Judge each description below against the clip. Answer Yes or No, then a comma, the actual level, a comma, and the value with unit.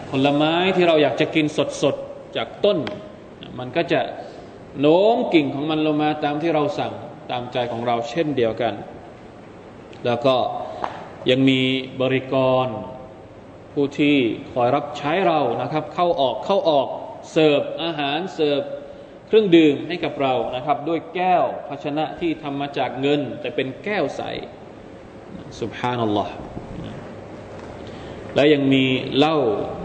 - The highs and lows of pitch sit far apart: No, average, 3.2 semitones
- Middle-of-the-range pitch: Yes, medium, 145 Hz